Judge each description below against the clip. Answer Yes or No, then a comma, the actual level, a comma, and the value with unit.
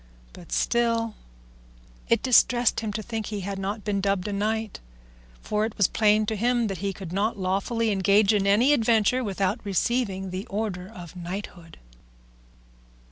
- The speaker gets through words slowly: No, average, 155 wpm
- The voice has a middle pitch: No, high, 210 Hz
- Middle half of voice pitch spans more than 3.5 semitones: No, narrow, 2.6 semitones